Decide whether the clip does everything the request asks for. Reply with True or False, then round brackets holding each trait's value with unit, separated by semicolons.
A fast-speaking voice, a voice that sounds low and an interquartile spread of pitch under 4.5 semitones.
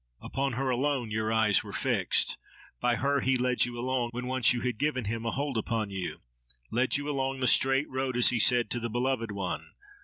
True (210 wpm; 125 Hz; 2.9 semitones)